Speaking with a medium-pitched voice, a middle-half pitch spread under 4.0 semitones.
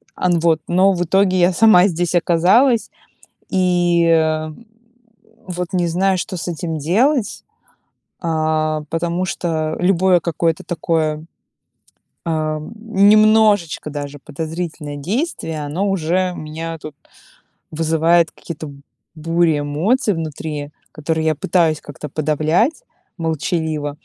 Yes: medium, 165 Hz; average, 2.7 semitones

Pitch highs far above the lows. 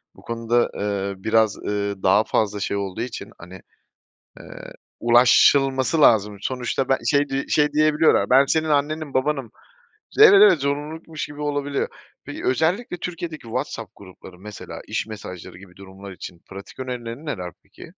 Yes: wide, 6.5 semitones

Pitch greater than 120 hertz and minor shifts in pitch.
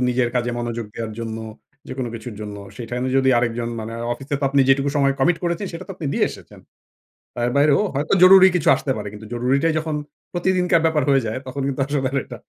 No: low, 135 Hz; average, 4.3 semitones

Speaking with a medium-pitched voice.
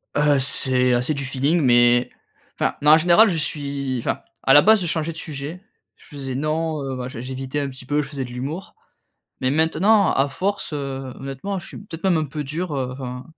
Yes: medium, 145 Hz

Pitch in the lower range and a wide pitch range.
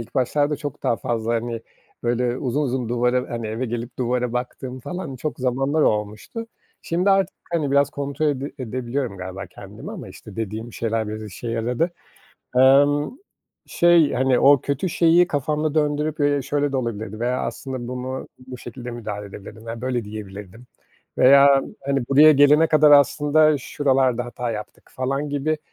No: low, 130 Hz; average, 3.5 semitones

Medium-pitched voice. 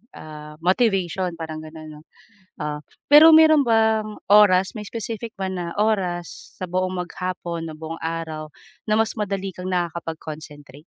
Yes: medium, 180 Hz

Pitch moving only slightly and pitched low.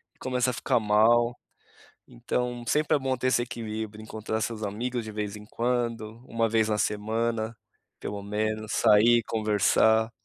Yes: narrow, 1.9 semitones; low, 110 Hz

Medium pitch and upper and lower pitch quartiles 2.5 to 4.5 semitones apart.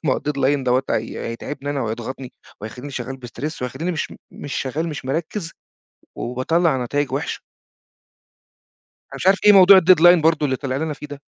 Yes: medium, 145 Hz; average, 4.0 semitones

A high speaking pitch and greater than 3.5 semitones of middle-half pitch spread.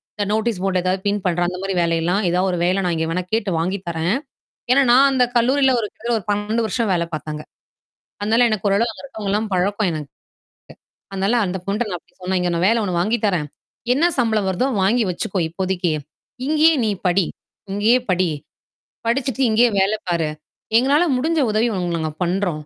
Yes: high, 200 Hz; average, 4.4 semitones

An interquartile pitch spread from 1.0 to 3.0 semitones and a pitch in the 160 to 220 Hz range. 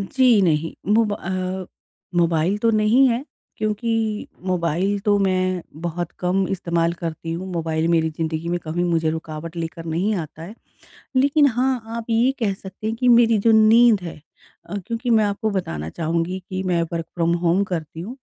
No: average, 4.6 semitones; medium, 185 Hz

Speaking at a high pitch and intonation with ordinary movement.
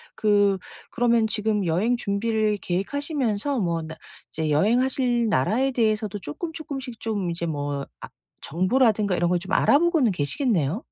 No: high, 210 Hz; wide, 5.7 semitones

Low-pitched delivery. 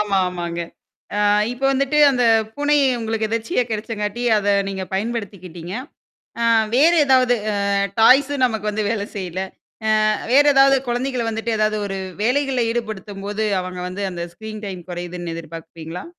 No: high, 215 Hz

